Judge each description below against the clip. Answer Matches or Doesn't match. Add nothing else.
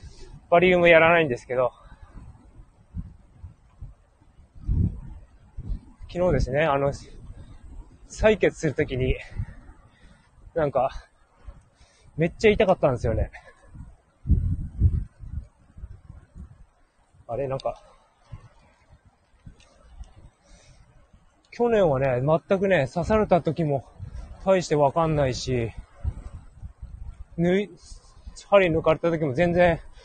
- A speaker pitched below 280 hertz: Matches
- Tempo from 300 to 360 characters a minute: Doesn't match